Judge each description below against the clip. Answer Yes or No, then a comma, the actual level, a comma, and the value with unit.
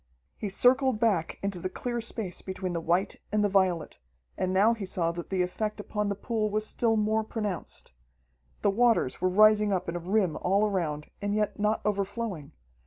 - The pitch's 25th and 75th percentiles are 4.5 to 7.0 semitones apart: No, average, 2.8 semitones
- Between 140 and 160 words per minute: No, average, 190 wpm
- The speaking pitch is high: Yes, high, 205 Hz